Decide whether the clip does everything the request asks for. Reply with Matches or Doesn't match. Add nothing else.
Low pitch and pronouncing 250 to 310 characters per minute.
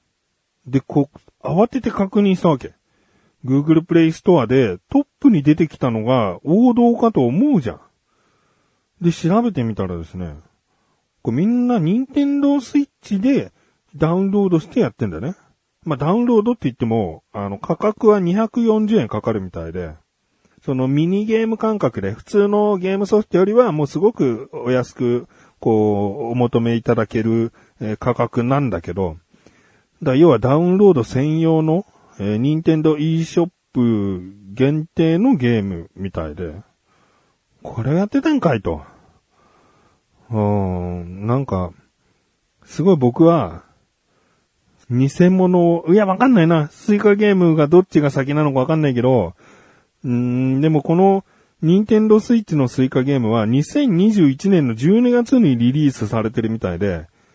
Doesn't match